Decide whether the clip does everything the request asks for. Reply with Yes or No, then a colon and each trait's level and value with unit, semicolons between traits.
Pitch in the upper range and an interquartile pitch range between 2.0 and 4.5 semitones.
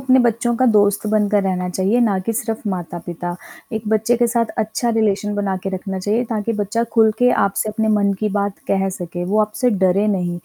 Yes: high, 210 Hz; average, 2.7 semitones